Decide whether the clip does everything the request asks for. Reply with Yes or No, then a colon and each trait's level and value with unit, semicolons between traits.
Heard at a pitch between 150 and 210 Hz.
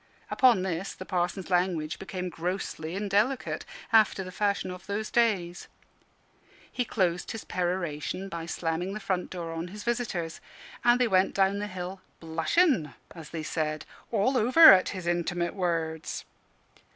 Yes: medium, 185 Hz